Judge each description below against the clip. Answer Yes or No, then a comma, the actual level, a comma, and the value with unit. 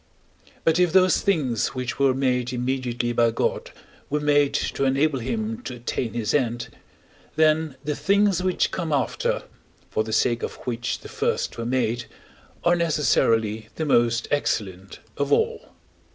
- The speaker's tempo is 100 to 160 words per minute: Yes, average, 150 wpm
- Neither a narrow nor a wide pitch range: Yes, average, 4.7 semitones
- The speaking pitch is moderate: No, low, 130 Hz